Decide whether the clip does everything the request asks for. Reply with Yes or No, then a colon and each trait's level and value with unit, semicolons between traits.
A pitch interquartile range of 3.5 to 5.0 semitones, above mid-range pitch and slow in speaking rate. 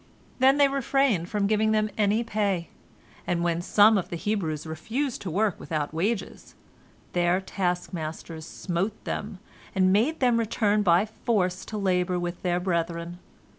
No: average, 3.9 semitones; high, 195 Hz; average, 150 wpm